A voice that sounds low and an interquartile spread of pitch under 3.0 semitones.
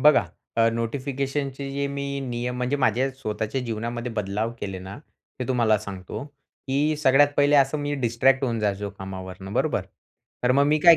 No: low, 125 Hz; average, 4.4 semitones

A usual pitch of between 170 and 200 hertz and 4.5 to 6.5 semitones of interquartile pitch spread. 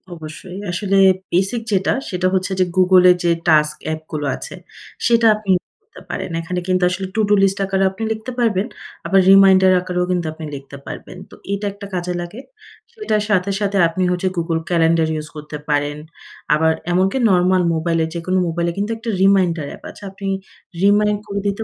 No: medium, 185 Hz; average, 3.0 semitones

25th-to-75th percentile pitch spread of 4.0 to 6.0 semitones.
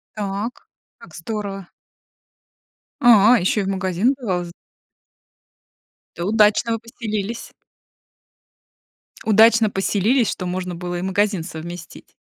No: average, 3.6 semitones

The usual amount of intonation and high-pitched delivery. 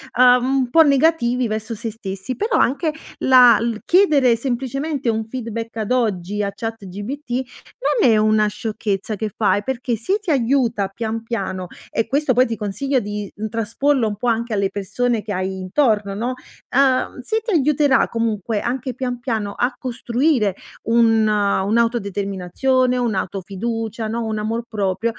Yes: average, 3.3 semitones; high, 230 Hz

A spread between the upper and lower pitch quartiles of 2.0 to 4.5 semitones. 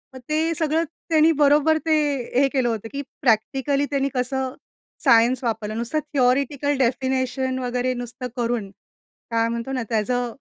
Yes: average, 3.0 semitones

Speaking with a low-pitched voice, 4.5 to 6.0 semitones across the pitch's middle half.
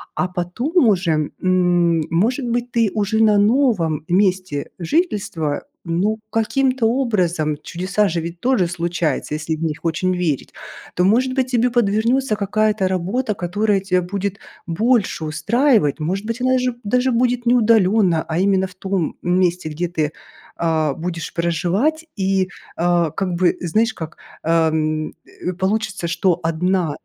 No: medium, 185 Hz; average, 4.8 semitones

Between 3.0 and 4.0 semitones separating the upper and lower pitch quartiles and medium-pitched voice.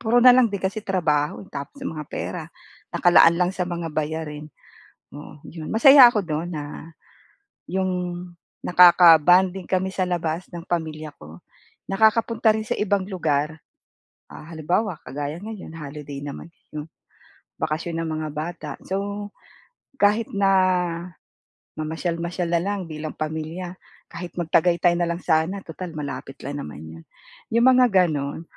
Yes: average, 3.6 semitones; medium, 170 Hz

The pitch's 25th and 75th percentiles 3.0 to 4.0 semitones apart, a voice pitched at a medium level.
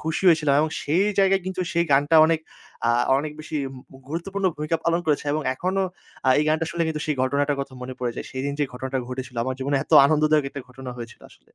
Yes: average, 3.6 semitones; medium, 150 Hz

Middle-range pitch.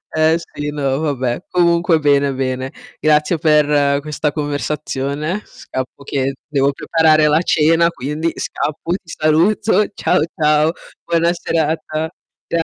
Yes: medium, 150 Hz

